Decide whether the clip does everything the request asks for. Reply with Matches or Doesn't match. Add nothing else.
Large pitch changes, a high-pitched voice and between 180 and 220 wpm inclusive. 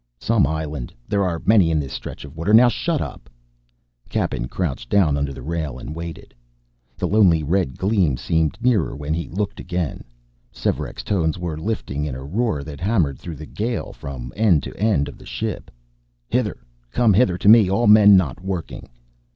Doesn't match